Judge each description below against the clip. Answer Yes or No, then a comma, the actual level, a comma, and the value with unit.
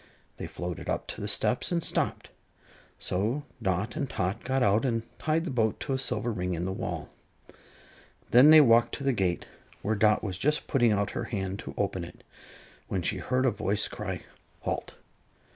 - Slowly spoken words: No, average, 190 wpm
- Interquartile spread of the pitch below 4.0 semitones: No, wide, 5.4 semitones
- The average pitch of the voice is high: No, low, 110 Hz